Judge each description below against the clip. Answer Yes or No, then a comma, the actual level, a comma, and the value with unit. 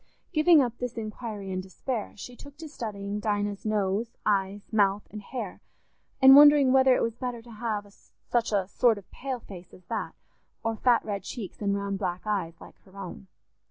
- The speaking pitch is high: Yes, high, 215 Hz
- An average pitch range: Yes, average, 3.7 semitones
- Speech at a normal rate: Yes, average, 190 wpm